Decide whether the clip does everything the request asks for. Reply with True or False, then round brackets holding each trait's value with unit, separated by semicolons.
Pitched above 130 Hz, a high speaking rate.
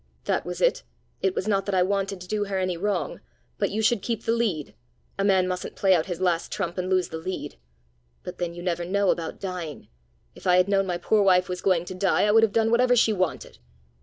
True (190 Hz; 245 wpm)